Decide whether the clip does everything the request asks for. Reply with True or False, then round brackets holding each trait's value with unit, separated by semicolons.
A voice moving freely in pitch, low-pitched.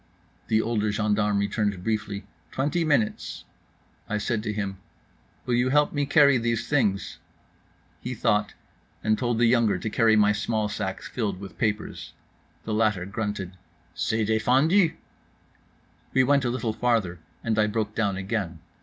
False (2.7 semitones; 110 Hz)